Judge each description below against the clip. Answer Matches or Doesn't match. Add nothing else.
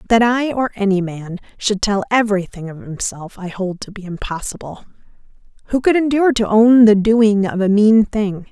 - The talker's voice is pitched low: Doesn't match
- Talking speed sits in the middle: Matches